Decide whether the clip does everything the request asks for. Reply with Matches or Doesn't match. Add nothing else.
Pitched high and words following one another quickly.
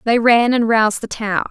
Matches